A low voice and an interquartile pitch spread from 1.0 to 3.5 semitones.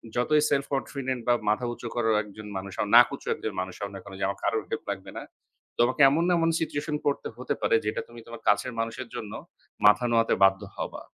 No: low, 120 Hz; average, 4.3 semitones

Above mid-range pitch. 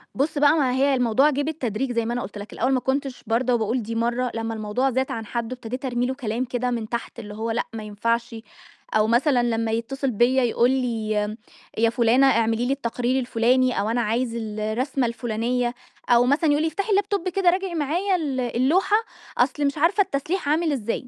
Yes: high, 245 Hz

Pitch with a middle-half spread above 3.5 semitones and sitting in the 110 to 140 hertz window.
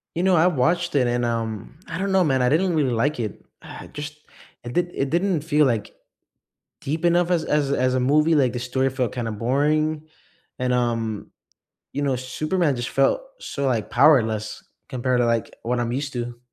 Yes: average, 4.4 semitones; low, 135 Hz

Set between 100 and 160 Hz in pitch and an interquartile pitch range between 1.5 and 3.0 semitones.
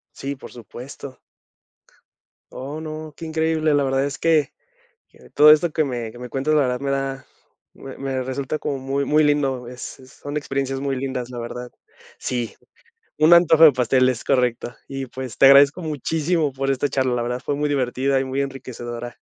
Yes: low, 135 Hz; narrow, 2.5 semitones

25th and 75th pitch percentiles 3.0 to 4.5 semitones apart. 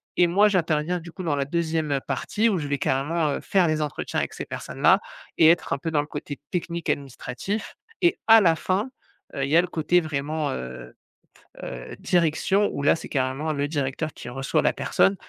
Yes: average, 3.6 semitones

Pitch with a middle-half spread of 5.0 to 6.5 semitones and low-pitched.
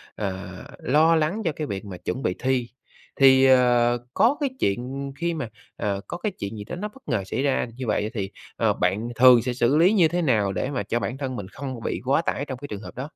Yes: wide, 5.5 semitones; low, 130 Hz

